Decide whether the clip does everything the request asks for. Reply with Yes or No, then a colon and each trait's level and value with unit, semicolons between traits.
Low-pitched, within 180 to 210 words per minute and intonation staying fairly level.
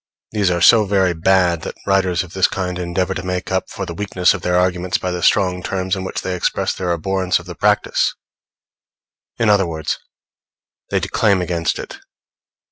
Yes: very low, 90 Hz; average, 190 wpm; narrow, 1.4 semitones